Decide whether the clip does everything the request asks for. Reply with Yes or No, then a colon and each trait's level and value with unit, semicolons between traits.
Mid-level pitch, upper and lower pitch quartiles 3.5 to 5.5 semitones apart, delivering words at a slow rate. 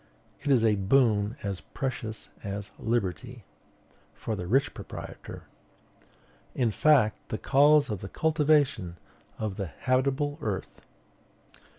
No: low, 115 Hz; average, 5.2 semitones; slow, 115 wpm